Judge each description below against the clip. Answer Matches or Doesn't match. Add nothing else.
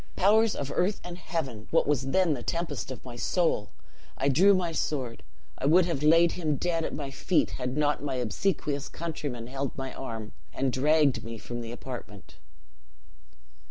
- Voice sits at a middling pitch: Matches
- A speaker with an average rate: Matches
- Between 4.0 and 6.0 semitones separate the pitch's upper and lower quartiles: Matches